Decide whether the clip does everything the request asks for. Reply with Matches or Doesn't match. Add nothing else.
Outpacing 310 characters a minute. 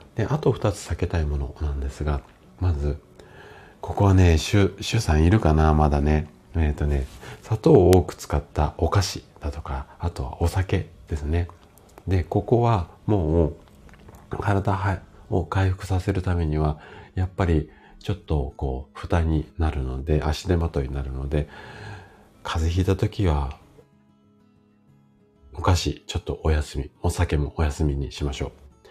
Doesn't match